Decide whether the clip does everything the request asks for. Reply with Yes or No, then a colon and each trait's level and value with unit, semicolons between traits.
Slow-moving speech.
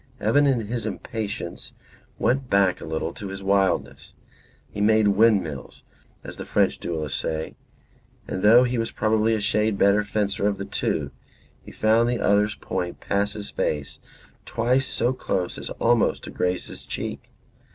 No: average, 165 wpm